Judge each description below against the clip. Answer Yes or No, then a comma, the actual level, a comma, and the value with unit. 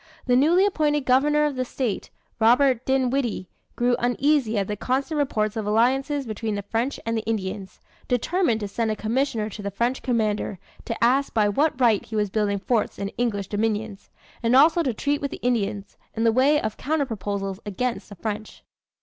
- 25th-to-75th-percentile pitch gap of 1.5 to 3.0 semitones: No, average, 4.2 semitones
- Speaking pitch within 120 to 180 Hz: No, high, 230 Hz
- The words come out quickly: No, average, 185 wpm